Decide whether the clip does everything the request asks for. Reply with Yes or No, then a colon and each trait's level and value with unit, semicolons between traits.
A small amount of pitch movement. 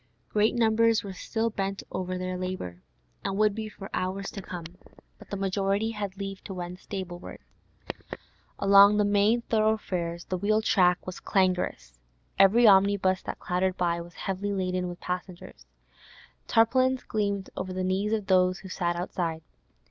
Yes: narrow, 2.3 semitones